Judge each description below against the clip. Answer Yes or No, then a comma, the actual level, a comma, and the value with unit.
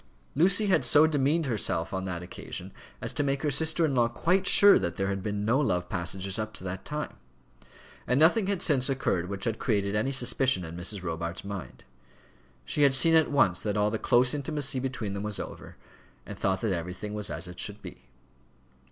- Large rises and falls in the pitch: Yes, wide, 7.0 semitones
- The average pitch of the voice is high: No, low, 110 Hz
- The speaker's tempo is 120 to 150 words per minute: No, fast, 205 wpm